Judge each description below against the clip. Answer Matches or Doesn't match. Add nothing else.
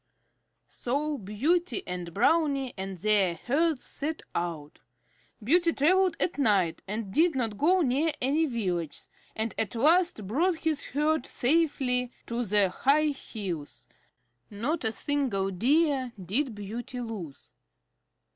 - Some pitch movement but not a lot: Doesn't match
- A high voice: Matches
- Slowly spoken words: Matches